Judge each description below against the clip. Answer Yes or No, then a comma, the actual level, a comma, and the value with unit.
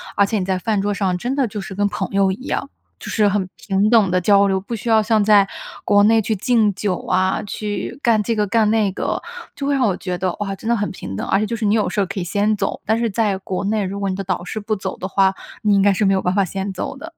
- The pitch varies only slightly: Yes, narrow, 2.2 semitones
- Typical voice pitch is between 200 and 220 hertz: Yes, high, 205 Hz